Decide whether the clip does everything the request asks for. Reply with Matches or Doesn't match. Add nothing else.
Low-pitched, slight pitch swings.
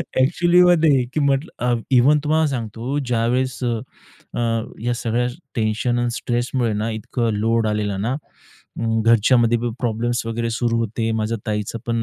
Matches